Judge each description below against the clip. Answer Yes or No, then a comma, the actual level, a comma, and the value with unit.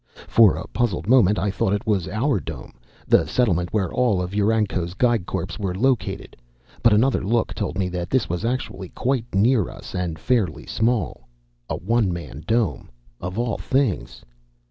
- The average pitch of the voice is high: No, low, 105 Hz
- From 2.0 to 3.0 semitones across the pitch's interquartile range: No, average, 4.7 semitones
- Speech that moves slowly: No, average, 170 wpm